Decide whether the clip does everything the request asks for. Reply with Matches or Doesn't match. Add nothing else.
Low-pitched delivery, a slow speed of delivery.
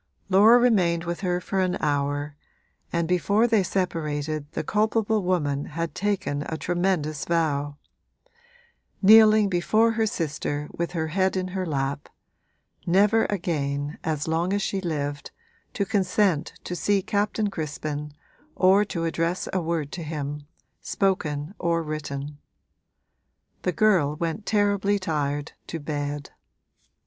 Doesn't match